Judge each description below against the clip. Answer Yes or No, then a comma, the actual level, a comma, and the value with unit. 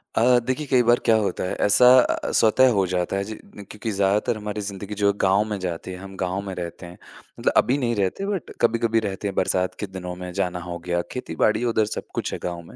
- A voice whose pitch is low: Yes, low, 100 Hz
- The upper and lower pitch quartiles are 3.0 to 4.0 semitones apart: Yes, average, 3.7 semitones